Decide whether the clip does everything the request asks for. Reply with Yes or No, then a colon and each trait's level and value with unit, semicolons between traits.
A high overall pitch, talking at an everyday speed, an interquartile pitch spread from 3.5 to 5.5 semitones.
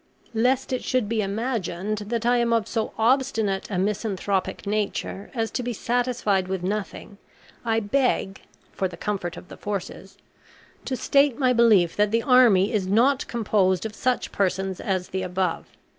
Yes: high, 215 Hz; average, 165 wpm; average, 3.8 semitones